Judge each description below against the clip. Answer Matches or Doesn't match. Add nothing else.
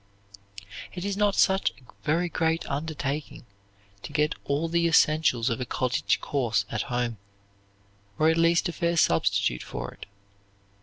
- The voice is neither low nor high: Matches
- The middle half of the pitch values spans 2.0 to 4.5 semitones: Doesn't match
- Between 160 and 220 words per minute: Doesn't match